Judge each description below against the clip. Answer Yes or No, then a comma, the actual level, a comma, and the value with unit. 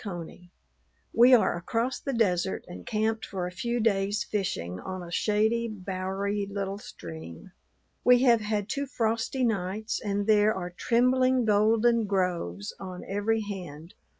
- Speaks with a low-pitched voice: No, high, 205 Hz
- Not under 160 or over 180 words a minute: No, average, 145 wpm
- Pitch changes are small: No, average, 3.6 semitones